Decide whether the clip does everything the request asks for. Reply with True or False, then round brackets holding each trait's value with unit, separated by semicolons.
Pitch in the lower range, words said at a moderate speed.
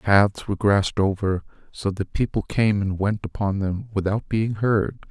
True (100 Hz; 190 wpm)